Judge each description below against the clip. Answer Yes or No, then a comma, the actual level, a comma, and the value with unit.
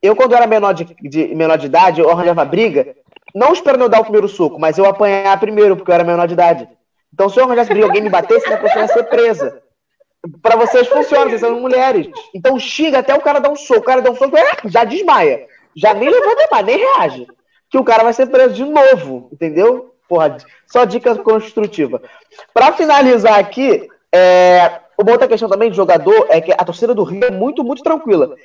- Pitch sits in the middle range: No, high, 235 Hz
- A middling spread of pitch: No, wide, 6.6 semitones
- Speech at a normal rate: No, fast, 215 wpm